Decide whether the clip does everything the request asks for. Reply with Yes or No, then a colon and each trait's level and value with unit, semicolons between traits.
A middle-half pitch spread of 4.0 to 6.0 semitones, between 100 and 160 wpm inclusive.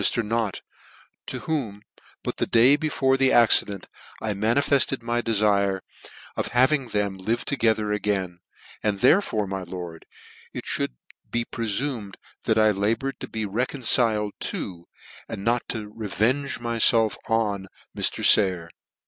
No: average, 3.1 semitones; average, 140 wpm